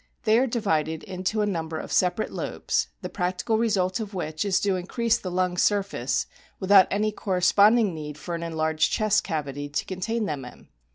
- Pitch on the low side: No, medium, 185 Hz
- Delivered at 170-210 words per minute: Yes, average, 180 wpm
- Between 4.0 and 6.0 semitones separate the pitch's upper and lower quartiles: Yes, average, 4.7 semitones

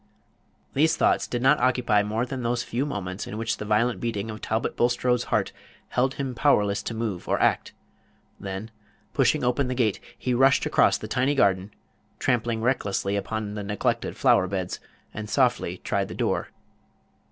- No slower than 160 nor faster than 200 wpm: Yes, average, 170 wpm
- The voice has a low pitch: Yes, low, 115 Hz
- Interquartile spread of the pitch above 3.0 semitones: Yes, average, 3.4 semitones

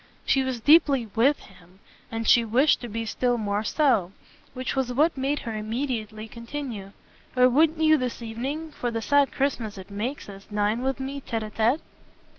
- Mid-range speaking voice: No, high, 240 Hz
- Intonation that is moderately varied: Yes, average, 4.1 semitones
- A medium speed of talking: Yes, average, 185 wpm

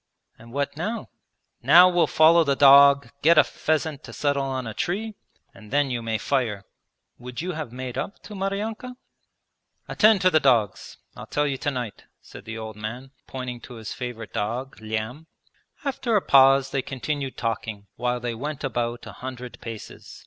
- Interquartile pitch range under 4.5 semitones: No, average, 4.8 semitones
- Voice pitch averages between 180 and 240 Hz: No, low, 135 Hz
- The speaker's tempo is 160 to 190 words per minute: Yes, average, 175 wpm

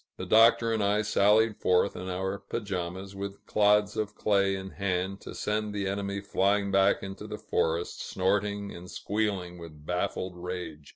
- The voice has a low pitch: Yes, low, 100 Hz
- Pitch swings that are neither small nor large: No, narrow, 2.1 semitones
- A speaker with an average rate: Yes, average, 165 wpm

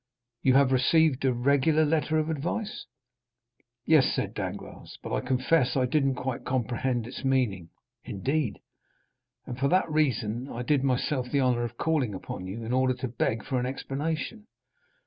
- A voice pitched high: No, low, 130 Hz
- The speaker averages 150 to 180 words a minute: Yes, average, 165 wpm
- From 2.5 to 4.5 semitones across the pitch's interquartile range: Yes, average, 3.5 semitones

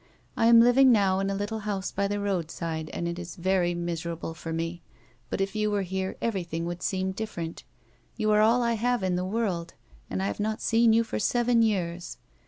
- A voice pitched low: No, high, 195 Hz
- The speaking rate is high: Yes, fast, 210 wpm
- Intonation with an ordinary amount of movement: Yes, average, 4.2 semitones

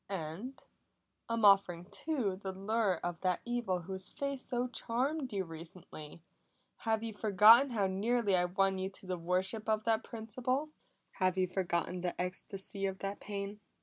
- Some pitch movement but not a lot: Yes, average, 3.7 semitones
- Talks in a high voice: Yes, high, 195 Hz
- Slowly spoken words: No, average, 160 wpm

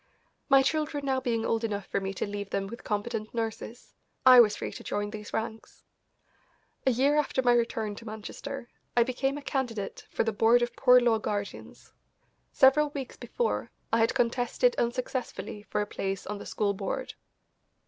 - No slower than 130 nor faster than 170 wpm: No, average, 180 wpm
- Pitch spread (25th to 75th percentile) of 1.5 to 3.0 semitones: No, average, 3.8 semitones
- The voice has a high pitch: Yes, high, 235 Hz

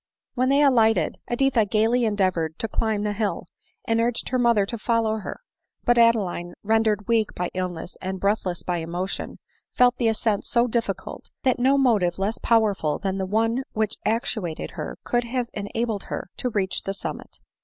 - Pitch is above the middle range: Yes, high, 220 Hz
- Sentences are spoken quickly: No, average, 175 wpm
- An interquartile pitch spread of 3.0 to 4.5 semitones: Yes, average, 3.5 semitones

